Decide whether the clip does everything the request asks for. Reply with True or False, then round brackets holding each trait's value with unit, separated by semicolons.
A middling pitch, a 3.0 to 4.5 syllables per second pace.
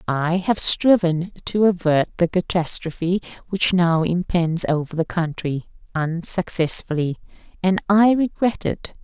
True (175 Hz; 4.1 syllables/s)